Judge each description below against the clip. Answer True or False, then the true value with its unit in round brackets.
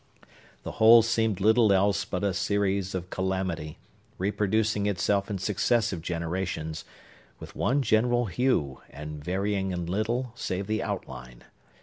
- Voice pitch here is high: False (100 Hz)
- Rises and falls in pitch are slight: False (3.3 semitones)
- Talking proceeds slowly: True (130 wpm)